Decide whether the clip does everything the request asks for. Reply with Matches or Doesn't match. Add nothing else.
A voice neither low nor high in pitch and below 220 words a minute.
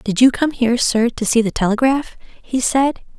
Doesn't match